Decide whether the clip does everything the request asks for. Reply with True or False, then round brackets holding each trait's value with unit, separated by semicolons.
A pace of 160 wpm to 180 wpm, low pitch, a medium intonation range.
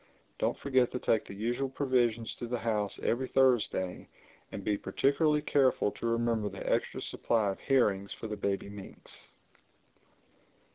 False (150 wpm; 115 Hz; 4.0 semitones)